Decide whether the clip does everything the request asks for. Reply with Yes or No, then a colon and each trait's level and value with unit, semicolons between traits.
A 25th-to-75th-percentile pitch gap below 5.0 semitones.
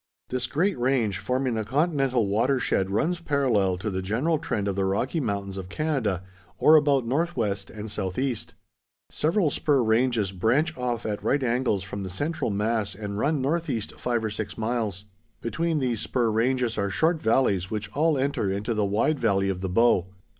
No: wide, 5.4 semitones